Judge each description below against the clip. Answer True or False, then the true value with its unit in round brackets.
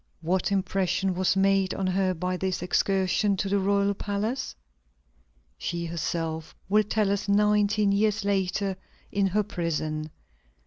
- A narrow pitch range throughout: True (1.8 semitones)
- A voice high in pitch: True (195 Hz)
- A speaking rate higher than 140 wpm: False (135 wpm)